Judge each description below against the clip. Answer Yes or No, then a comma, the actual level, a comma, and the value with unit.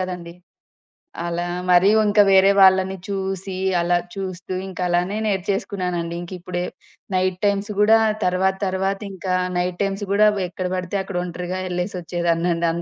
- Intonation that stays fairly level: Yes, narrow, 1.6 semitones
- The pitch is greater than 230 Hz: No, medium, 185 Hz